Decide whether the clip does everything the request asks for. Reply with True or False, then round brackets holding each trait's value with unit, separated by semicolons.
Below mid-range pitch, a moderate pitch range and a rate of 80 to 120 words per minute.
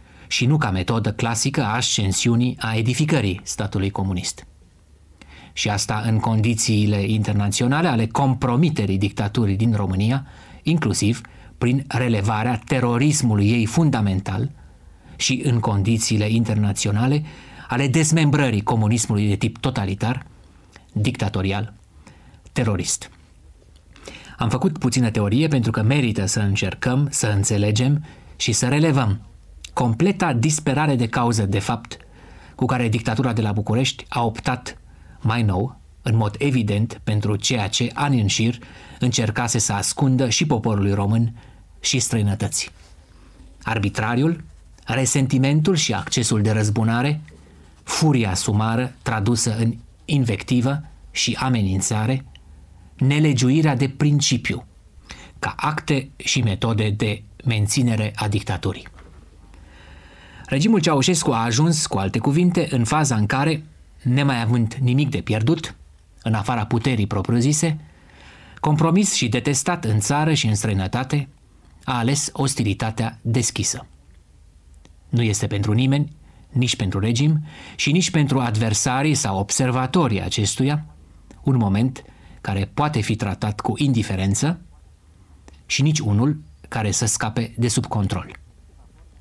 True (115 Hz; 4.7 semitones; 115 wpm)